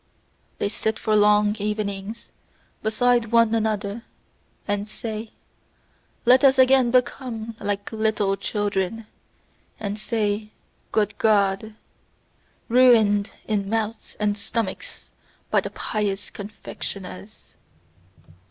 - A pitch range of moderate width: No, narrow, 1.8 semitones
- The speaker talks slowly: Yes, slow, 95 wpm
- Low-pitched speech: No, high, 215 Hz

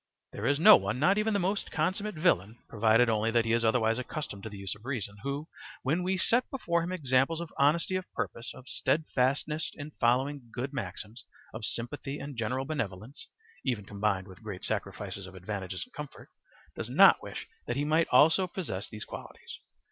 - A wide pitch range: Yes, wide, 6.3 semitones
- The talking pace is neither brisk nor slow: Yes, average, 190 wpm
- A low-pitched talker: Yes, low, 130 Hz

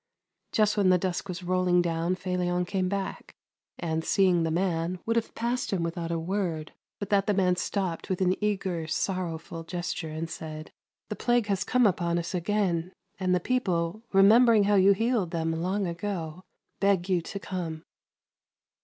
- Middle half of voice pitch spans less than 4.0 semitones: Yes, average, 2.8 semitones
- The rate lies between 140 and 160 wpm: No, average, 180 wpm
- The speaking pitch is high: No, medium, 180 Hz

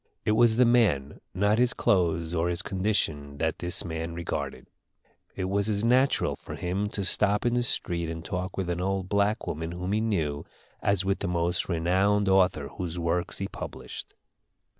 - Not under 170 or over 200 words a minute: Yes, average, 180 wpm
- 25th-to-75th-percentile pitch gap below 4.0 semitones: Yes, average, 3.5 semitones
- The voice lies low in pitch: Yes, very low, 95 Hz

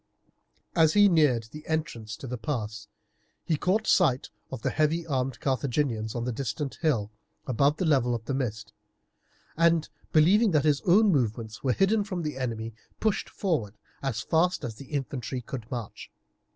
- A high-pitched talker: No, low, 135 Hz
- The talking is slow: No, average, 165 wpm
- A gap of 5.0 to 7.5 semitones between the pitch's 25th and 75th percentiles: Yes, wide, 5.6 semitones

